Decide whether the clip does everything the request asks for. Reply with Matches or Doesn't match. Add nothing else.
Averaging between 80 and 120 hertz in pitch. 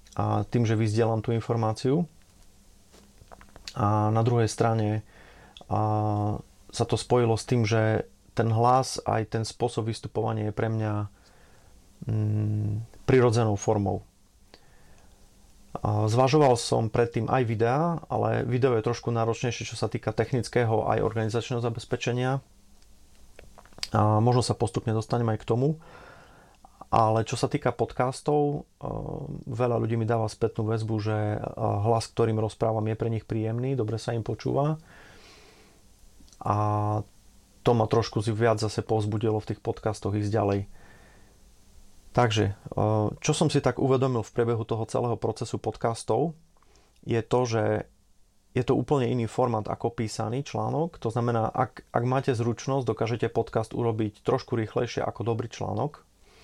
Matches